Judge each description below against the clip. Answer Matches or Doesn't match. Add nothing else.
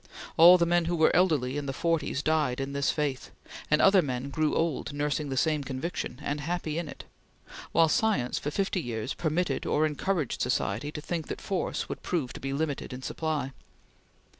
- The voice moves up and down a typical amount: Matches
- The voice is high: Doesn't match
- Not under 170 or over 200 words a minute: Matches